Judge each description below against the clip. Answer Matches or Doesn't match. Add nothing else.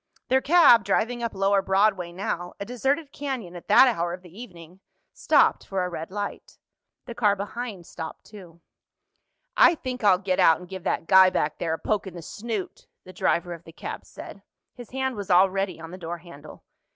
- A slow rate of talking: Doesn't match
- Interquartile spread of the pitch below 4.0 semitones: Doesn't match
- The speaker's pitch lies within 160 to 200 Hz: Matches